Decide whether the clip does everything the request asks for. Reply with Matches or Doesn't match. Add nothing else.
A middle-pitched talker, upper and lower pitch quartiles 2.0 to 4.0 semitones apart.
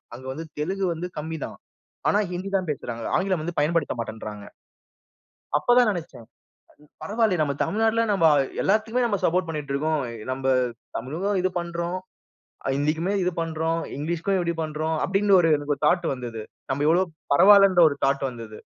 Doesn't match